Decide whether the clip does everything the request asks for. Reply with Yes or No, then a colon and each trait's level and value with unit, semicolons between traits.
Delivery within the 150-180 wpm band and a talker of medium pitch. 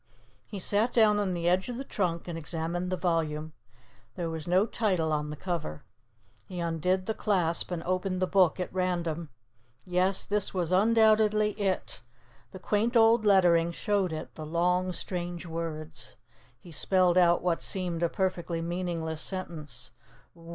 Yes: average, 160 wpm; medium, 180 Hz